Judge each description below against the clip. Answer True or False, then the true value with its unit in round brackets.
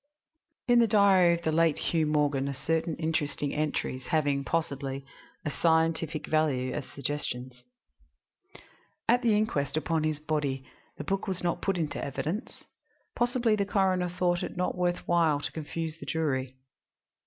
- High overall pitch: False (160 Hz)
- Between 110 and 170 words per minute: True (155 wpm)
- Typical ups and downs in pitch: True (3.6 semitones)